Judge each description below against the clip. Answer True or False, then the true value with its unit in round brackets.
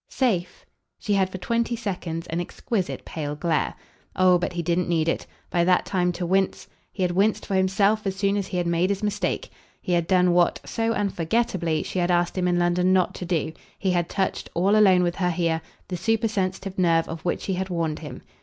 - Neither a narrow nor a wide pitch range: False (2.1 semitones)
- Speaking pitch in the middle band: True (180 Hz)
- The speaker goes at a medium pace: False (220 wpm)